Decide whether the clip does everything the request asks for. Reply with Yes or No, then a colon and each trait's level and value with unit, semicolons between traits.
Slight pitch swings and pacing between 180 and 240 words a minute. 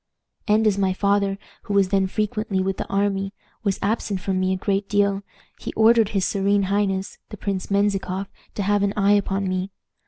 Yes: narrow, 1.0 semitones; average, 190 wpm